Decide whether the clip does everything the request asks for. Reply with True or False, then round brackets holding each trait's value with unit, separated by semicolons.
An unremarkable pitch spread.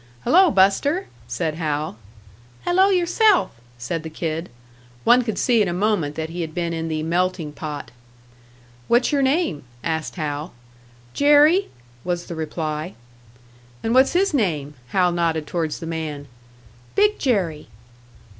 False (8.4 semitones)